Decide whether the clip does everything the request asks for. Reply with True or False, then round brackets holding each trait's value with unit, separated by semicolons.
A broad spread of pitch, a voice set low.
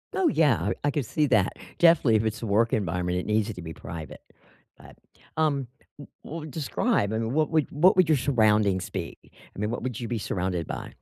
True (6.8 semitones; 115 Hz)